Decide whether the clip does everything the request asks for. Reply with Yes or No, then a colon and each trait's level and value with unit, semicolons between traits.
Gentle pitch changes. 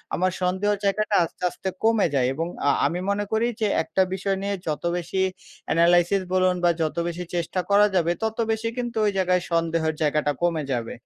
No: average, 3.3 semitones